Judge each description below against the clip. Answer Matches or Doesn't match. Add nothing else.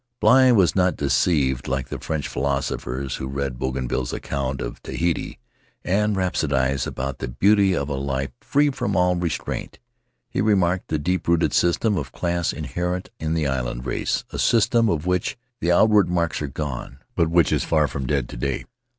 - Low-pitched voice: Matches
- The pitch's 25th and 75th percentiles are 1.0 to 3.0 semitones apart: Doesn't match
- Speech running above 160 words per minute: Matches